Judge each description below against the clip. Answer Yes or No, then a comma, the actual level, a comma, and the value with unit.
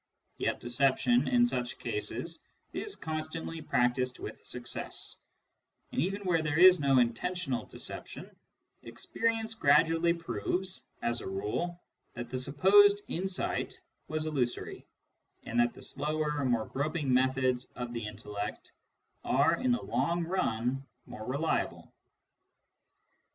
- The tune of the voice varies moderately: No, wide, 6.3 semitones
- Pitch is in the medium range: Yes, medium, 145 Hz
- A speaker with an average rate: No, slow, 120 wpm